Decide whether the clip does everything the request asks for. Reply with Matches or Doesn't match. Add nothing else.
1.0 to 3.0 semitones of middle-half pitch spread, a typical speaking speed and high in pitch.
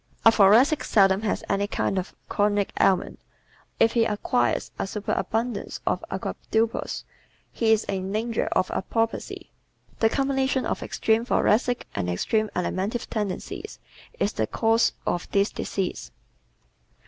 Doesn't match